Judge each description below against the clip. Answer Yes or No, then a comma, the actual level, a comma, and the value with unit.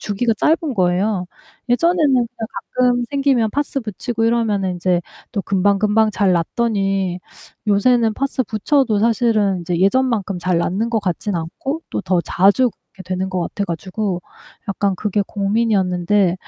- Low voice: No, high, 205 Hz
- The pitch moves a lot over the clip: No, average, 3.9 semitones